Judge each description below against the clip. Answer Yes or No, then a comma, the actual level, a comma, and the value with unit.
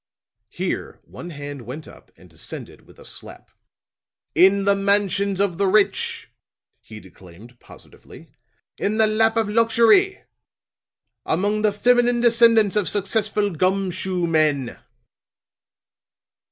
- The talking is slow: Yes, slow, 120 wpm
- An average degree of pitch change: Yes, average, 4.6 semitones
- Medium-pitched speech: No, high, 200 Hz